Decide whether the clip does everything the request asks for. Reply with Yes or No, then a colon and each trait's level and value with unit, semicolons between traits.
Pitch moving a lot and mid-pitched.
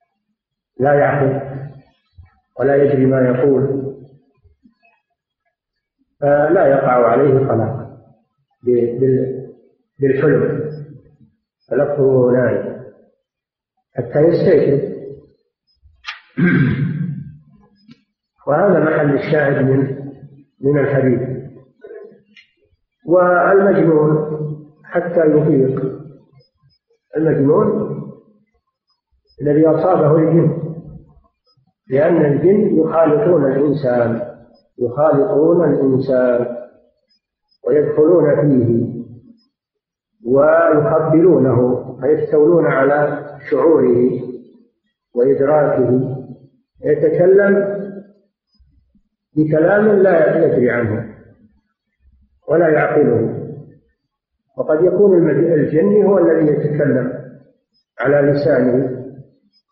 Yes: wide, 6.2 semitones; medium, 145 Hz